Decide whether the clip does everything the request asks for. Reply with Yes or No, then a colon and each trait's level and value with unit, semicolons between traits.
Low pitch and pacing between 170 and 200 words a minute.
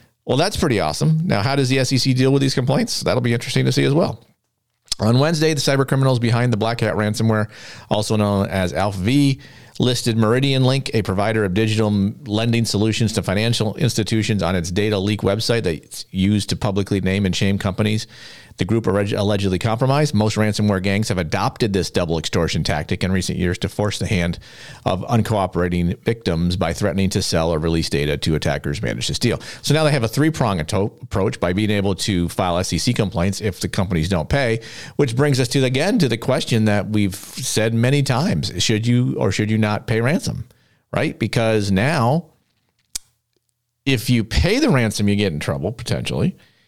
Yes: low, 110 Hz; average, 190 wpm